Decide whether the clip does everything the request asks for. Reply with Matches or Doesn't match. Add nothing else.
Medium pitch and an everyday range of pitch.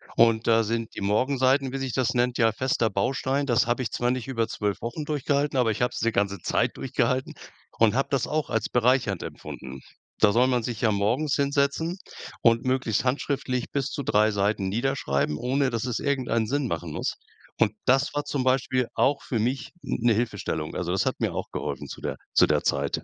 Doesn't match